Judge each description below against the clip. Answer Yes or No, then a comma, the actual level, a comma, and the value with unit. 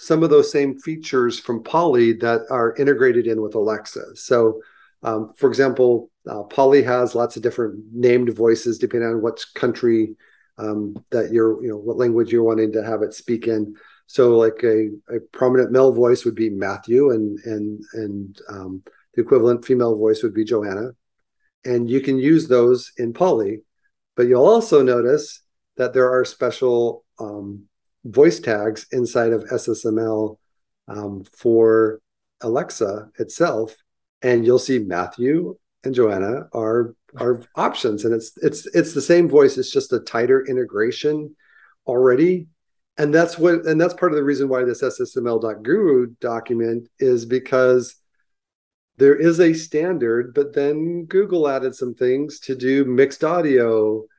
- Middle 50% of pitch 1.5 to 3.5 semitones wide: No, average, 4.2 semitones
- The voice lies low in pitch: Yes, low, 120 Hz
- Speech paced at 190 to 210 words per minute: No, average, 155 wpm